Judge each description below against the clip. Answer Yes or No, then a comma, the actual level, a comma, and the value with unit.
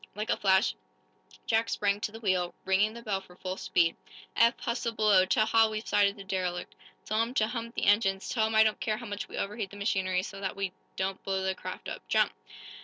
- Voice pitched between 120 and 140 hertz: No, high, 205 Hz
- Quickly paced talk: Yes, fast, 230 wpm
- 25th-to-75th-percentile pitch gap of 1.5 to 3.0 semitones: Yes, narrow, 2.4 semitones